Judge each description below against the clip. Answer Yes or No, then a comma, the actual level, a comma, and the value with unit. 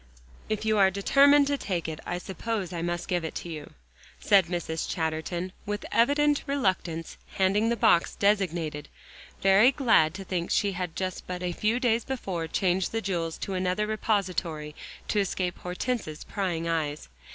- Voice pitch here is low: No, medium, 185 Hz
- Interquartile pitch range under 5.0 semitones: Yes, average, 4.1 semitones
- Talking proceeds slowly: No, average, 165 wpm